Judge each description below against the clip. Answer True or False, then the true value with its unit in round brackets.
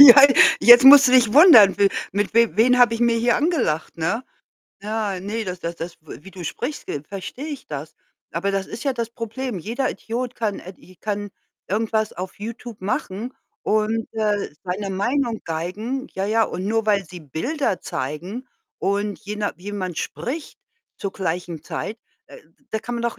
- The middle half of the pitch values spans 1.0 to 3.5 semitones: False (4.2 semitones)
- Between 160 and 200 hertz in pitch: False (215 Hz)